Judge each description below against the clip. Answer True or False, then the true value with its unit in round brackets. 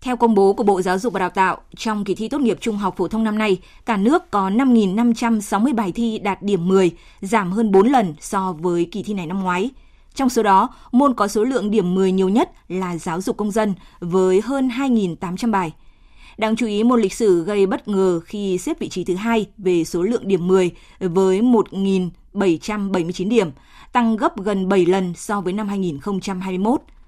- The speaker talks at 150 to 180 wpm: False (205 wpm)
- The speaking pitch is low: False (200 Hz)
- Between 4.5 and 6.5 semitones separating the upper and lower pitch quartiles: False (3.7 semitones)